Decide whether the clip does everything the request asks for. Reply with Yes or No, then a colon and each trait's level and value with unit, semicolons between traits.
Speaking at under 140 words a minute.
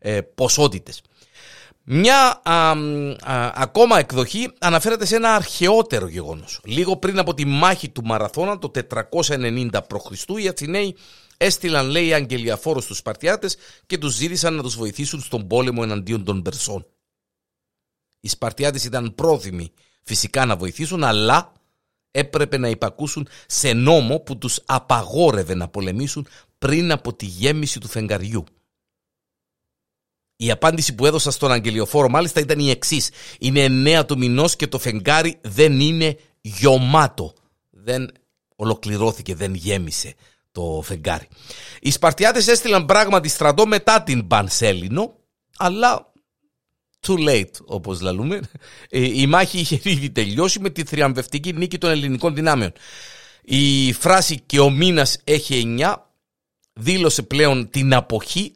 Yes: average, 130 wpm